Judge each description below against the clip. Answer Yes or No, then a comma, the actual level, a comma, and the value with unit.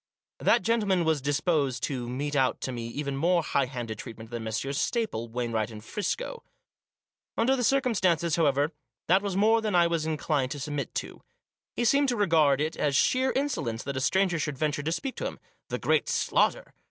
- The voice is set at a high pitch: No, medium, 150 Hz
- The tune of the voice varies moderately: No, wide, 7.2 semitones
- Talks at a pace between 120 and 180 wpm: No, average, 195 wpm